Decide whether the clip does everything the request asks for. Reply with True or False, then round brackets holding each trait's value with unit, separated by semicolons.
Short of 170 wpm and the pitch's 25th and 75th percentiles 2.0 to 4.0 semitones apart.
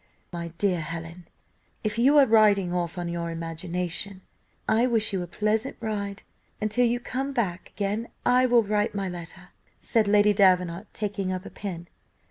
False (175 wpm; 3.7 semitones)